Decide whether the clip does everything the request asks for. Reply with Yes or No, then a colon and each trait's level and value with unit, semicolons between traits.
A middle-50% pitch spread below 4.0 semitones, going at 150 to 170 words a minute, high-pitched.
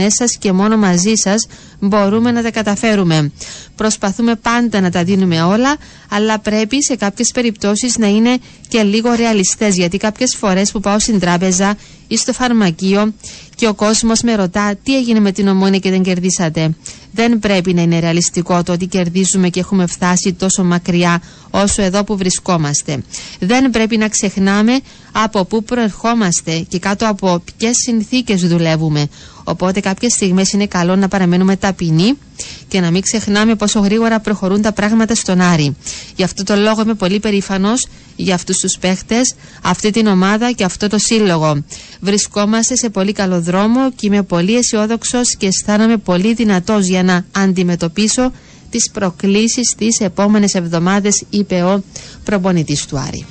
Yes: average, 3.0 semitones; average, 160 wpm; high, 200 Hz